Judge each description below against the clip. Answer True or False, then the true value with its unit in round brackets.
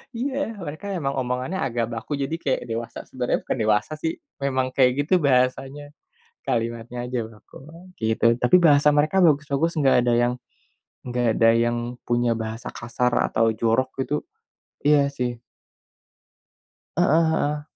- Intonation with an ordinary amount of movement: True (3.7 semitones)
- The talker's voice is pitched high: False (130 Hz)